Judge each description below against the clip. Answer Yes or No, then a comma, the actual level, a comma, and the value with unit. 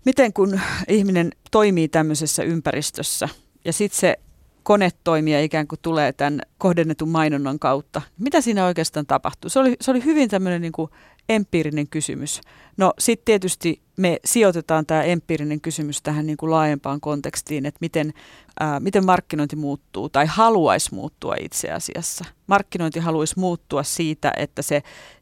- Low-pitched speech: No, medium, 160 Hz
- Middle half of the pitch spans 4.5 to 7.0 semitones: No, average, 4.0 semitones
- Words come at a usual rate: Yes, average, 145 wpm